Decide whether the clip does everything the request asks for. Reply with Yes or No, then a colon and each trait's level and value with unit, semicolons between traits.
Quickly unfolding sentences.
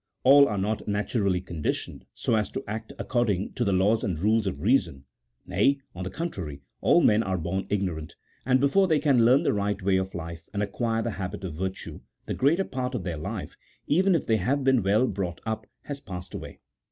Yes: fast, 210 wpm